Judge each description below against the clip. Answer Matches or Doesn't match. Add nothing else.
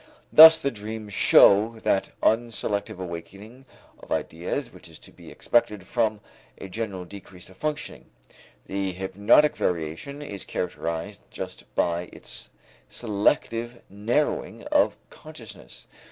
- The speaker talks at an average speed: Doesn't match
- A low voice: Matches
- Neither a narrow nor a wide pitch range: Matches